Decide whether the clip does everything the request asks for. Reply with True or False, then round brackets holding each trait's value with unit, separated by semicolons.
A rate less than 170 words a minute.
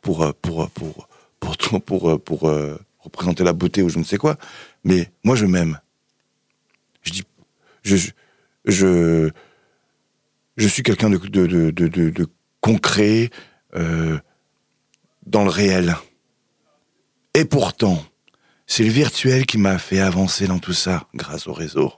True (145 wpm)